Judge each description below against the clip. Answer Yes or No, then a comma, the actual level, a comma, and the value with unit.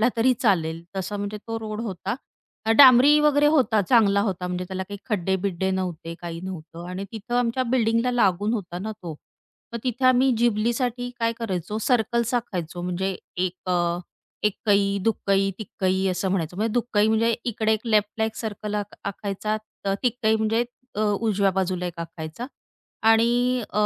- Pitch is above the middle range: Yes, high, 210 Hz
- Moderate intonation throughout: Yes, average, 3.5 semitones